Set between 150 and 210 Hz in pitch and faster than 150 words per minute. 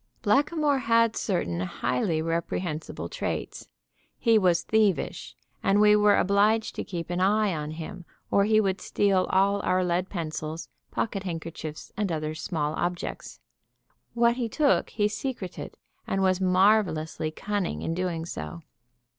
No: medium, 185 Hz; average, 140 wpm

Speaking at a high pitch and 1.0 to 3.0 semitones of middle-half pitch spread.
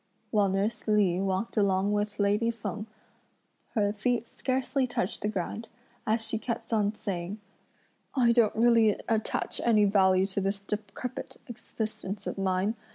Yes: high, 210 Hz; narrow, 2.5 semitones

